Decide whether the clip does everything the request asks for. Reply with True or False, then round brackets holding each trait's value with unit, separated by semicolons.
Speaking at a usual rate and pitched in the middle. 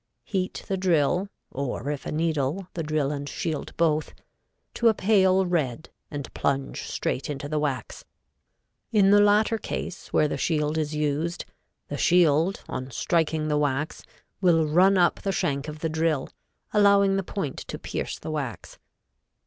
True (160 wpm; 160 Hz)